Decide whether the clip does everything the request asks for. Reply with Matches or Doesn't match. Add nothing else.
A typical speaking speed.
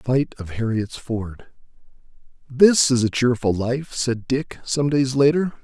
Matches